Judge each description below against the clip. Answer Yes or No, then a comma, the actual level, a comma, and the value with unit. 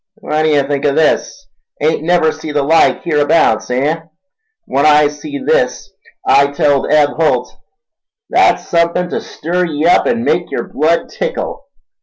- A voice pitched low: No, medium, 155 Hz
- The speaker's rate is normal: Yes, average, 150 wpm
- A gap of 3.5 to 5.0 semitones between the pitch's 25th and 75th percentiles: No, average, 2.7 semitones